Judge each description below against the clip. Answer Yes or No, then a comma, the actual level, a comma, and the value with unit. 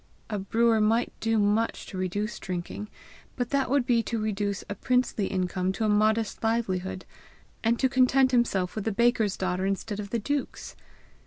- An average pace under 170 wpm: No, average, 175 wpm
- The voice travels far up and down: No, average, 3.2 semitones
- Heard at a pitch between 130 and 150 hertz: No, high, 215 Hz